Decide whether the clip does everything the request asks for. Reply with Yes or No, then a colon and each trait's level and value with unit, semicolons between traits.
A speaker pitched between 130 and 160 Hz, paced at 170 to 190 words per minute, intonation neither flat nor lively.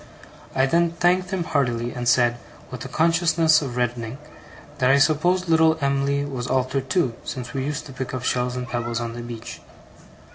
Yes: low, 135 Hz; average, 185 wpm; average, 4.6 semitones